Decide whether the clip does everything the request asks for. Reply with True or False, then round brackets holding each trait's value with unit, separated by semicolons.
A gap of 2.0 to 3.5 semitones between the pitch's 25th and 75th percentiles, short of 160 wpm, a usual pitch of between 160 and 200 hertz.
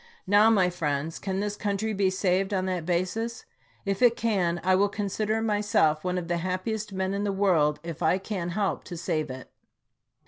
False (2.9 semitones; 200 wpm; 190 Hz)